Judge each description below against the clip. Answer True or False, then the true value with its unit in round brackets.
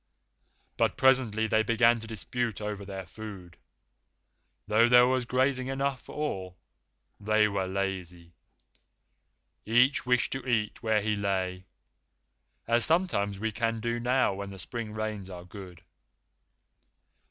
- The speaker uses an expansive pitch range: False (3.8 semitones)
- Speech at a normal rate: False (130 wpm)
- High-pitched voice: False (110 Hz)